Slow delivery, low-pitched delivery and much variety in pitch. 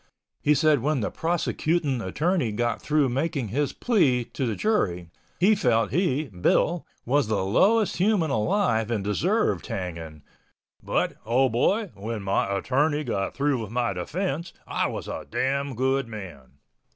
No: average, 150 wpm; low, 130 Hz; wide, 6.7 semitones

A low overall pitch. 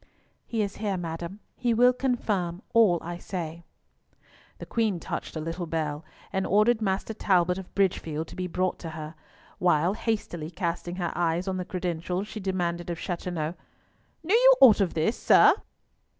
No: medium, 180 Hz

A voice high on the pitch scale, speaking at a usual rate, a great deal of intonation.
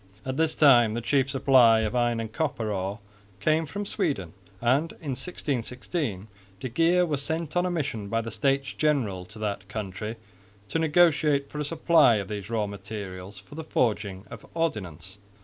No: low, 120 Hz; average, 175 wpm; wide, 6.5 semitones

